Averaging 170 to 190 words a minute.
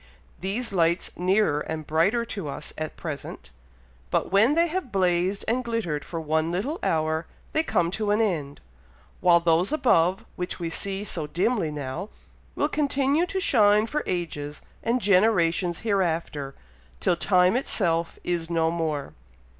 No: average, 150 wpm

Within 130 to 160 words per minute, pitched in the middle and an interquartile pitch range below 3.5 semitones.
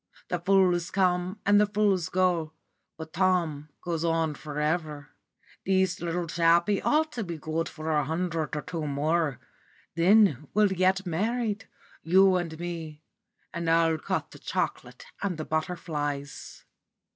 Yes: average, 145 wpm; medium, 170 Hz; average, 2.9 semitones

